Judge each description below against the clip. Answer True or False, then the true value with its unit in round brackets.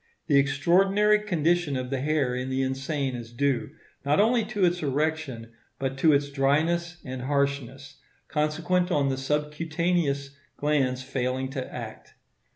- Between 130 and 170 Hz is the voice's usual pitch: True (140 Hz)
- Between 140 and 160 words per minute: True (145 wpm)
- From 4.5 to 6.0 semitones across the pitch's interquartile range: False (3.8 semitones)